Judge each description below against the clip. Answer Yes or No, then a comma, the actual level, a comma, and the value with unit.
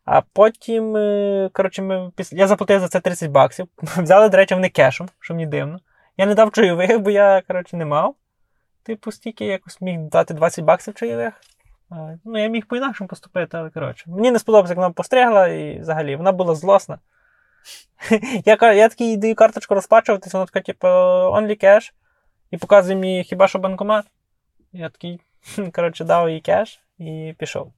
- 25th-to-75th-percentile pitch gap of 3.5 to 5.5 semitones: Yes, average, 3.8 semitones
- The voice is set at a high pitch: Yes, high, 195 Hz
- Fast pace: Yes, fast, 165 wpm